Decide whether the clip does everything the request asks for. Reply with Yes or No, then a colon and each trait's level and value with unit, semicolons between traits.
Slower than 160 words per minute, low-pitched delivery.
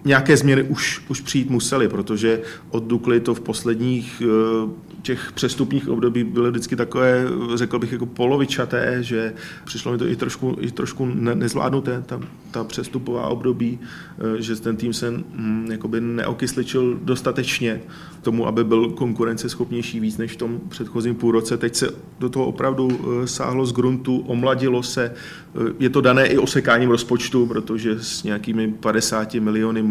Yes: average, 145 wpm; low, 120 Hz